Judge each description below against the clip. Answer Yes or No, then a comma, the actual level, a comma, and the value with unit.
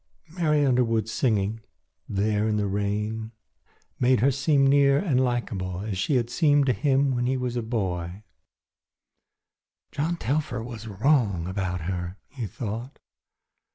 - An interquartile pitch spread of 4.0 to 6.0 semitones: Yes, average, 5.0 semitones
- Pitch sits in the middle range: No, low, 115 Hz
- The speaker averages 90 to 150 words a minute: Yes, average, 145 wpm